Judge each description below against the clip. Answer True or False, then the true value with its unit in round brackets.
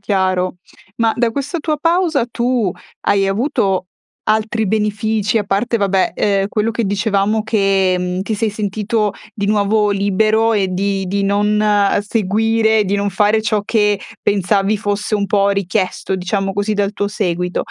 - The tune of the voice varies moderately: False (1.9 semitones)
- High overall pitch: True (205 Hz)